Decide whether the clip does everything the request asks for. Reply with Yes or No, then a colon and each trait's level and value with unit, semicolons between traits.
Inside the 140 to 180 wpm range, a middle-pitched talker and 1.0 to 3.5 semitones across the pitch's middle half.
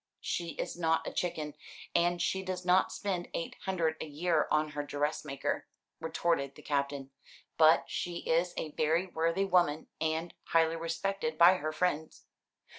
Yes: average, 155 wpm; medium, 165 Hz; narrow, 2.4 semitones